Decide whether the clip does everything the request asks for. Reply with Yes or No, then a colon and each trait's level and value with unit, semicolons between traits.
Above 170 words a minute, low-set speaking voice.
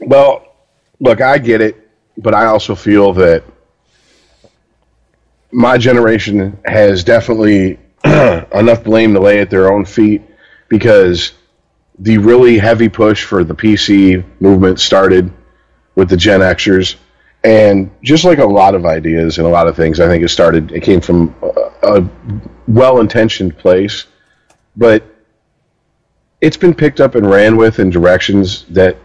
No: average, 145 wpm; low, 105 Hz